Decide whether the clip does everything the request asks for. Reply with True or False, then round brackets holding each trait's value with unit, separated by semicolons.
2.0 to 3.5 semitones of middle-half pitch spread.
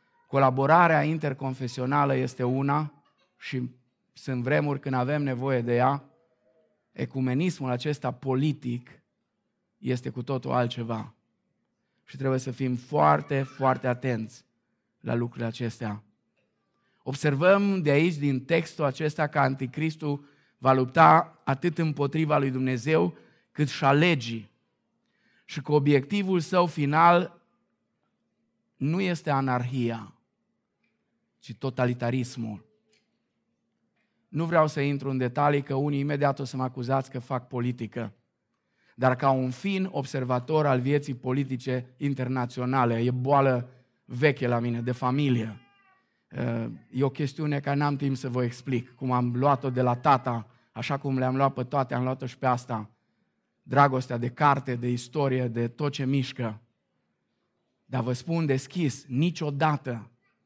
True (2.9 semitones)